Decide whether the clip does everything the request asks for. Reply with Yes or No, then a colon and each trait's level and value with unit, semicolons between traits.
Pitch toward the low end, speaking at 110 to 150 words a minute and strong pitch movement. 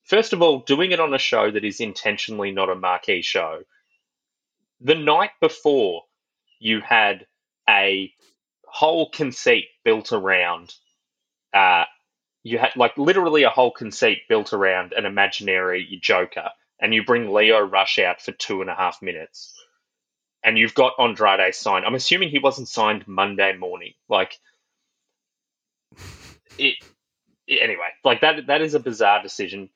Yes: low, 125 Hz; average, 145 wpm; wide, 7.9 semitones